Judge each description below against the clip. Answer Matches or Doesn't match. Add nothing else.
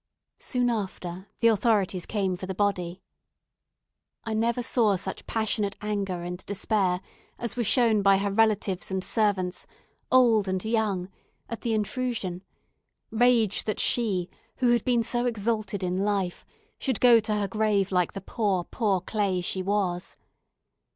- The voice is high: Matches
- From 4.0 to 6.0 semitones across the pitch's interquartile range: Doesn't match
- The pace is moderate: Matches